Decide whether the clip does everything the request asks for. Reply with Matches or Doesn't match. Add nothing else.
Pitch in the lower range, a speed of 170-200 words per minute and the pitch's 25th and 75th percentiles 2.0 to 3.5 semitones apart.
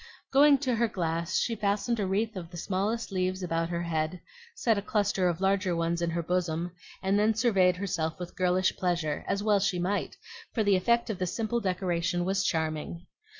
Doesn't match